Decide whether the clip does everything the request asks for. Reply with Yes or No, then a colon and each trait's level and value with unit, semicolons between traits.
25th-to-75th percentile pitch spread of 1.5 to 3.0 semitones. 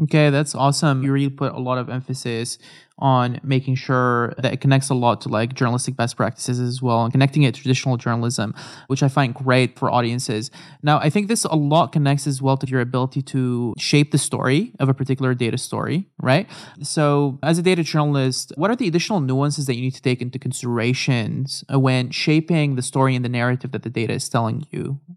Yes: average, 2.7 semitones